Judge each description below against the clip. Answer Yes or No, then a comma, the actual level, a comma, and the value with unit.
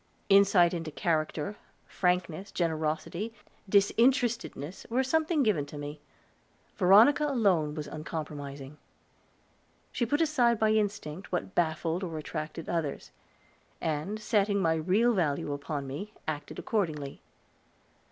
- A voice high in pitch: No, medium, 175 Hz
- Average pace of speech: No, slow, 110 wpm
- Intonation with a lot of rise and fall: Yes, wide, 5.7 semitones